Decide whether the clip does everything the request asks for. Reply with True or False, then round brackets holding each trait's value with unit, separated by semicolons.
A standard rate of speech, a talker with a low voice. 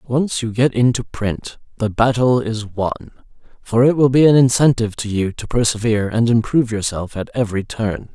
True (185 wpm; 115 Hz)